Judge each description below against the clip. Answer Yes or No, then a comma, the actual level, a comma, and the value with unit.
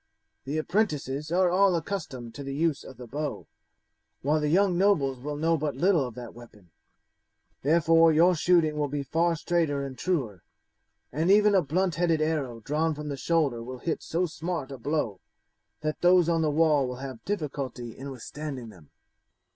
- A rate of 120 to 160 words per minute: No, average, 180 wpm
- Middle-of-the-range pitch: Yes, medium, 150 Hz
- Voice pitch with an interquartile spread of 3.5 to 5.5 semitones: Yes, average, 4.0 semitones